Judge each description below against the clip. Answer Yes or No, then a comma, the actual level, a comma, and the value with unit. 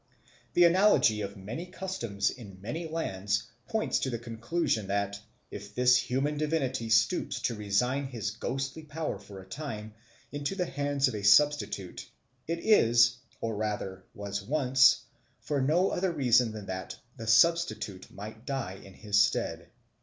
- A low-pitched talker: Yes, low, 120 Hz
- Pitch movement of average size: No, wide, 6.3 semitones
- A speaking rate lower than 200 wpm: Yes, average, 155 wpm